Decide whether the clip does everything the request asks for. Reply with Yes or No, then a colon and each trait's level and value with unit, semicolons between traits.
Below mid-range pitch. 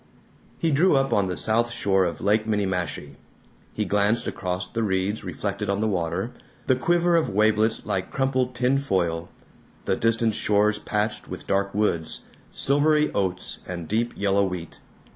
Yes: low, 105 Hz